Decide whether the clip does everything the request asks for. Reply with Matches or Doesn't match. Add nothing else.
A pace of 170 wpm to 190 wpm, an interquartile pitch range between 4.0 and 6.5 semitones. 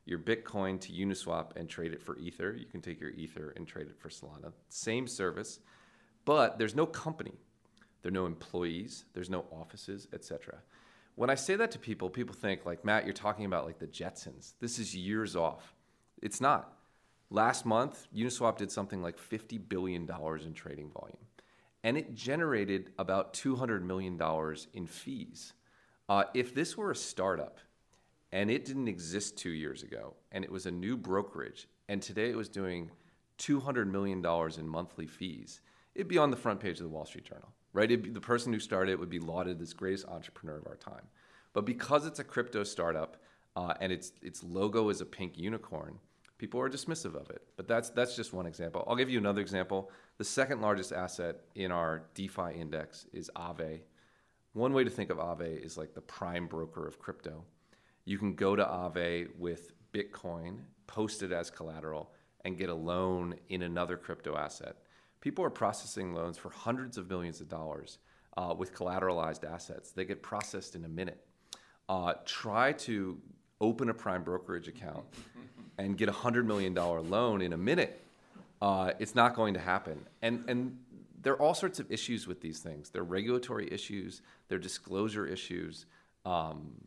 Matches